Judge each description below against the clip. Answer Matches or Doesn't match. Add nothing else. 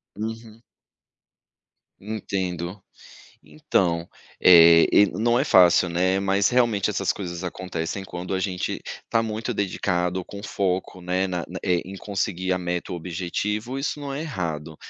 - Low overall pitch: Matches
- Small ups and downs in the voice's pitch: Doesn't match